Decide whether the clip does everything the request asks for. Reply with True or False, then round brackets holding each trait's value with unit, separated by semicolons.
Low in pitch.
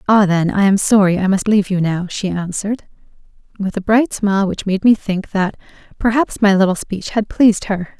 False (200 Hz)